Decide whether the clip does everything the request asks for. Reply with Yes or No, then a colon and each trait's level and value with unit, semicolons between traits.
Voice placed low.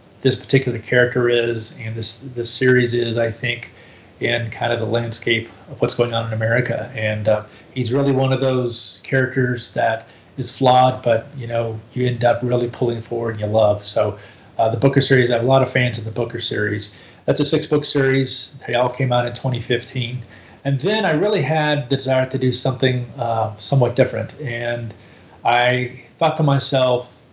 Yes: low, 120 Hz